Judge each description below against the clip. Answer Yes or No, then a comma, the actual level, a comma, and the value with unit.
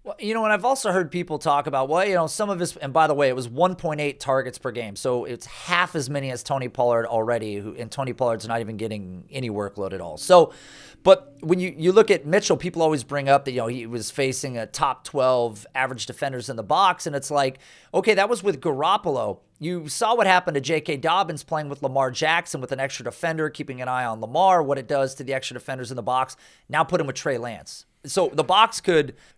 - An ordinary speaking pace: No, fast, 250 wpm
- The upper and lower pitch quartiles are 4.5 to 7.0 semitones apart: Yes, average, 5.1 semitones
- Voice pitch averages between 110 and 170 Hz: Yes, medium, 140 Hz